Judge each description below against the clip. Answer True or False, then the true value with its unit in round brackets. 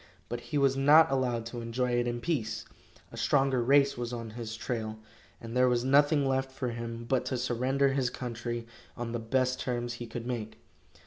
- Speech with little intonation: True (2.2 semitones)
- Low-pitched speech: True (125 Hz)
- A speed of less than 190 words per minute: False (195 wpm)